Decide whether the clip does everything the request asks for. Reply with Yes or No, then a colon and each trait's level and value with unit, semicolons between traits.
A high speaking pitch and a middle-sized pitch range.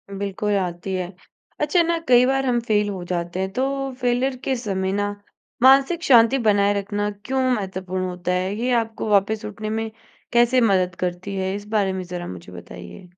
Yes: high, 205 Hz; average, 4.4 semitones